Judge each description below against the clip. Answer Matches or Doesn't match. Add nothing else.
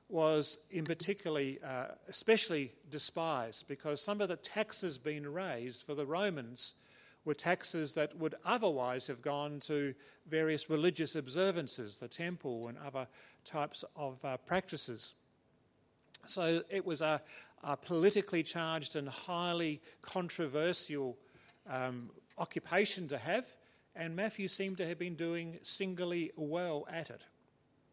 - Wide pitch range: Doesn't match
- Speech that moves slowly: Matches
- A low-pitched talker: Doesn't match